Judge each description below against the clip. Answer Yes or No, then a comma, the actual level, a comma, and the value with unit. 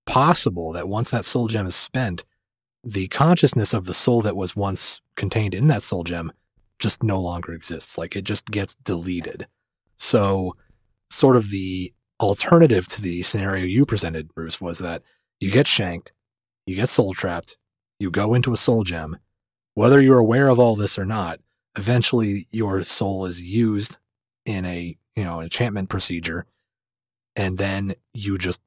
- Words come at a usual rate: Yes, average, 165 wpm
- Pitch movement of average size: Yes, average, 4.3 semitones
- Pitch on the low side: Yes, low, 100 Hz